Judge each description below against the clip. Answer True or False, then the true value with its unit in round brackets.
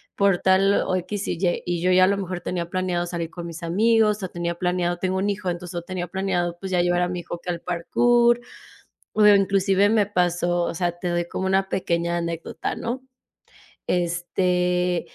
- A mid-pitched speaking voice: True (180 Hz)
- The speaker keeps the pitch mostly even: True (1.9 semitones)